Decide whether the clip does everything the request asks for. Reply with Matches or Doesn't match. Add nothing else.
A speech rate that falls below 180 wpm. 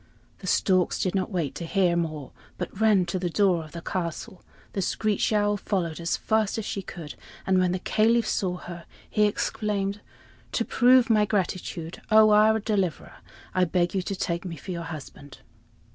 Doesn't match